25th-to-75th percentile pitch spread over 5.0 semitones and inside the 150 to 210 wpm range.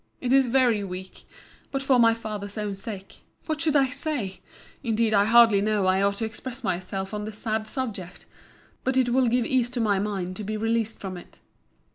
No: average, 3.8 semitones; average, 185 wpm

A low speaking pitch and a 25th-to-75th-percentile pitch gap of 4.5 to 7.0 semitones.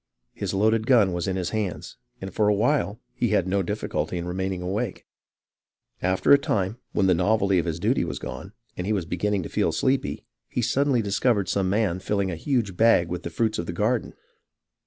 No: low, 100 Hz; average, 3.2 semitones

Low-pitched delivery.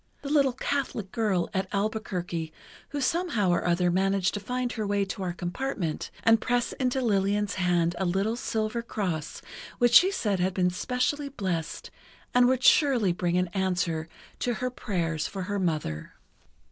No: high, 200 Hz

